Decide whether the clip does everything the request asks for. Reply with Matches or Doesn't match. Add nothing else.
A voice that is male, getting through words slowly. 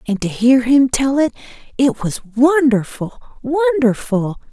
Doesn't match